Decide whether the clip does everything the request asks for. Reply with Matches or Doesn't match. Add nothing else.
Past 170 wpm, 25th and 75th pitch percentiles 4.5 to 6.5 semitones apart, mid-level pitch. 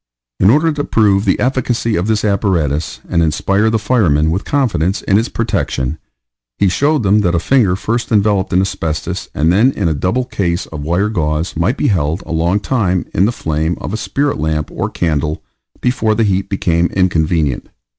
Doesn't match